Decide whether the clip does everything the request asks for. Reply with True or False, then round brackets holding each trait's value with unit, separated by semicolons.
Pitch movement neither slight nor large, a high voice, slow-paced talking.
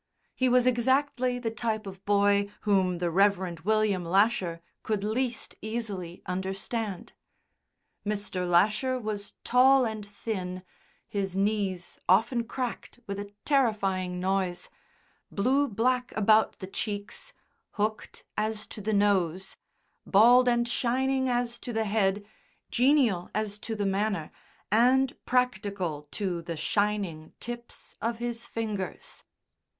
True (3.6 semitones; 210 Hz; 125 wpm)